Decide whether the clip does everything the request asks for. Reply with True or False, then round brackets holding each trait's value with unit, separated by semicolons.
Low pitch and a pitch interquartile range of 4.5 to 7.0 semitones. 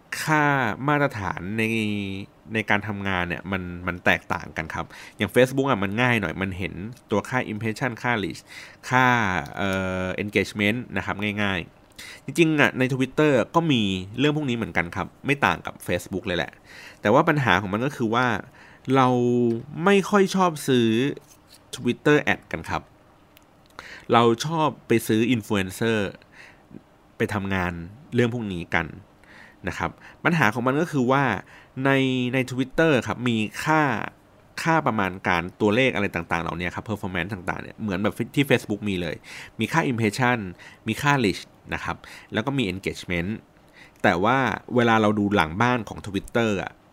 True (110 Hz; 5.0 semitones)